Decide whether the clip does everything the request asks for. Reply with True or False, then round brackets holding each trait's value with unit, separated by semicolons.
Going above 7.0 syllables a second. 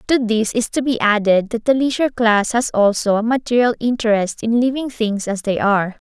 False (5.3 syllables/s)